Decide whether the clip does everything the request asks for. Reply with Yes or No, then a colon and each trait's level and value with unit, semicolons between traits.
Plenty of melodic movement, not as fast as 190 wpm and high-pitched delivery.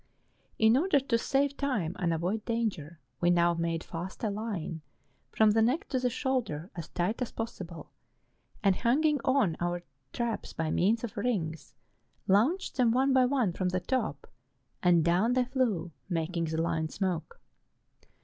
Yes: wide, 6.5 semitones; average, 160 wpm; high, 205 Hz